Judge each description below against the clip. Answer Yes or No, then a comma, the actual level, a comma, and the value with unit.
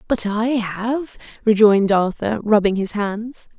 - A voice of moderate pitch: No, high, 215 Hz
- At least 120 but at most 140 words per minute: Yes, slow, 135 wpm